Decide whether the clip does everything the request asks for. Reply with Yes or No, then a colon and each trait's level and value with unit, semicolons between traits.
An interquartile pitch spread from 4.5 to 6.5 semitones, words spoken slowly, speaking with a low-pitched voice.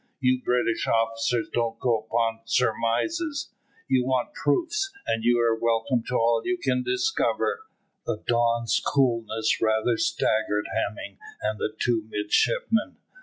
No: narrow, 2.4 semitones; slow, 130 wpm; low, 115 Hz